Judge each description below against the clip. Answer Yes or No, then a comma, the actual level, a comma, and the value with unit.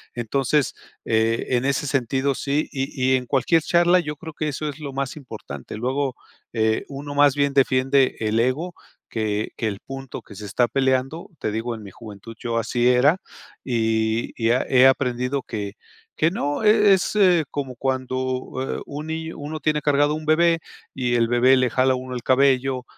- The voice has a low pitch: Yes, low, 130 Hz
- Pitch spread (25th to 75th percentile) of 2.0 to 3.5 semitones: Yes, average, 3.2 semitones